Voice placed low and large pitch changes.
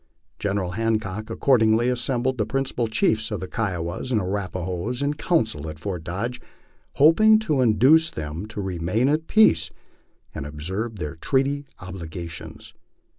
Yes: low, 110 Hz; wide, 6.2 semitones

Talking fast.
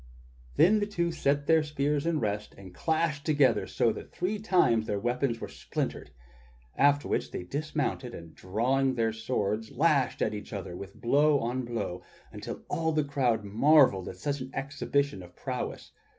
No: average, 170 wpm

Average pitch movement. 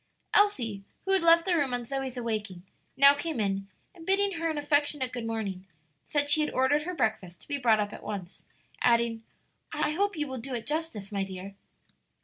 No: wide, 6.1 semitones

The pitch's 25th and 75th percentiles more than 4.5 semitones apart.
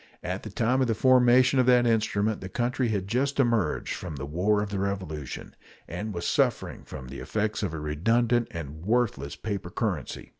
Yes: wide, 5.6 semitones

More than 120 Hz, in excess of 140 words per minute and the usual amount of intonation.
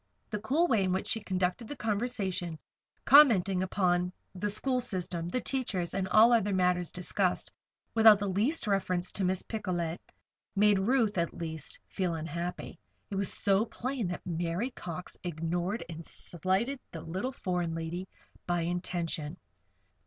Yes: medium, 185 Hz; average, 150 wpm; average, 3.6 semitones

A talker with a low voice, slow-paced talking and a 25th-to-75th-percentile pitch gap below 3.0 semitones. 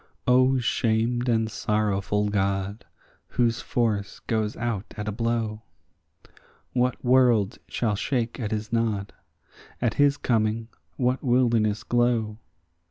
Yes: low, 115 Hz; slow, 115 wpm; narrow, 2.4 semitones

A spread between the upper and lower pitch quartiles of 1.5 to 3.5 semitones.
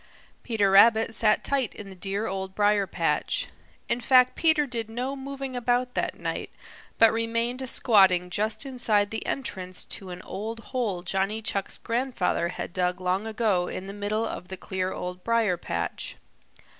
No: average, 4.0 semitones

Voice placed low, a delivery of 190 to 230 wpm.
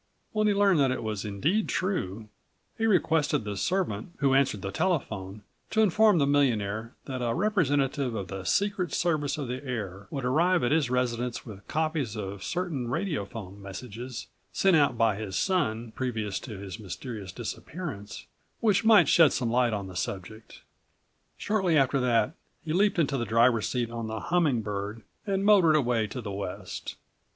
No: low, 125 Hz; average, 170 wpm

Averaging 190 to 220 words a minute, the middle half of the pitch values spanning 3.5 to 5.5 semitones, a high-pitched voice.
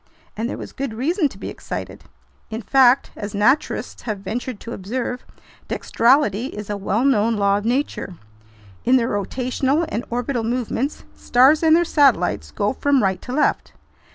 No: average, 165 wpm; average, 4.5 semitones; high, 245 Hz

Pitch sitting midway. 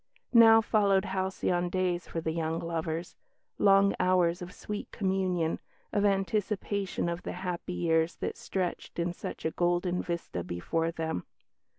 Yes: medium, 180 Hz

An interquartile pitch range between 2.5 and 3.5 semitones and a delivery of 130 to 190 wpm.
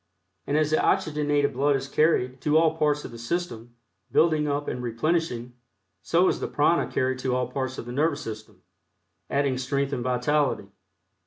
Yes: average, 3.2 semitones; average, 175 wpm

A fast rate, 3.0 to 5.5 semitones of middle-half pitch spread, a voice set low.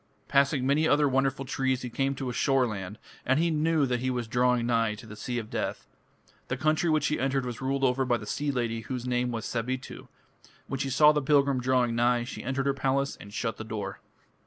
No: fast, 225 wpm; narrow, 2.4 semitones; low, 130 Hz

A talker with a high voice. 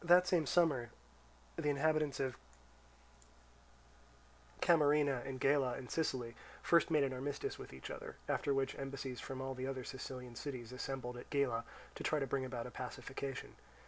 No: low, 135 Hz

